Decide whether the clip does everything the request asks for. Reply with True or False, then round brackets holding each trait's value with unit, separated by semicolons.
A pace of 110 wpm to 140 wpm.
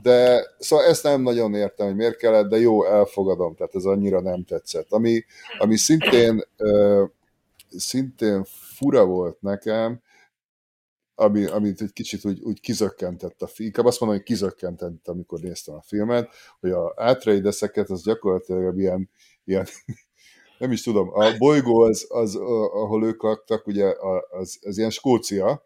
False (150 wpm)